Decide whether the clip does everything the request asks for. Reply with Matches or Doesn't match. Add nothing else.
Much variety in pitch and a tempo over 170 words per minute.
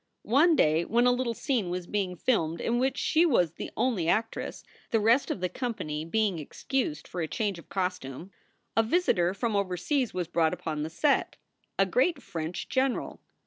Matches